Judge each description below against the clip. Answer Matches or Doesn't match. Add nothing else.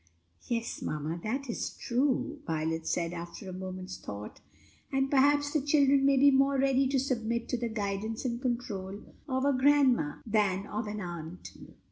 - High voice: Matches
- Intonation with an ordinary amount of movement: Doesn't match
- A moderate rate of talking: Matches